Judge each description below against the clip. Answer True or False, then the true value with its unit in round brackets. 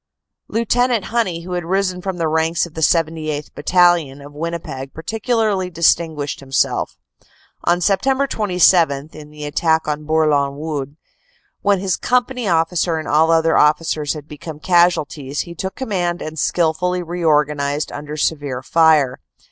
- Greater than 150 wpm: False (140 wpm)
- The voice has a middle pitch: True (165 Hz)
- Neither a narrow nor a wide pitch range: True (3.3 semitones)